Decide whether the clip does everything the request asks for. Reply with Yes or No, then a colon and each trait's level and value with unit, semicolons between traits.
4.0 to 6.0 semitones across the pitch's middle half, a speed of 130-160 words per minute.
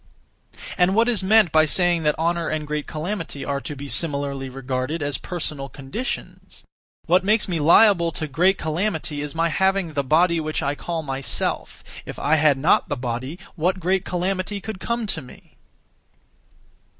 No: average, 4.3 semitones; average, 170 wpm